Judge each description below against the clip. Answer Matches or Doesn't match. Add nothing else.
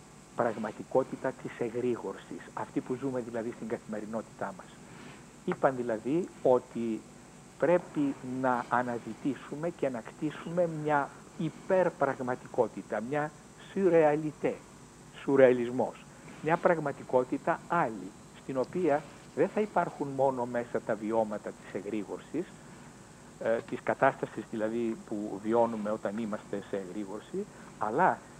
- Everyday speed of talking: Doesn't match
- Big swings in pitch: Doesn't match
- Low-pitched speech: Matches